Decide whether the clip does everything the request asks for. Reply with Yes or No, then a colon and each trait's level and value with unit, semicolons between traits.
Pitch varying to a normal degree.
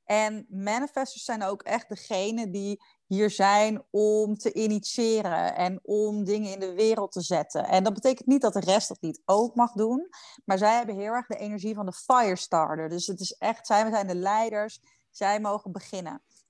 No: narrow, 2.3 semitones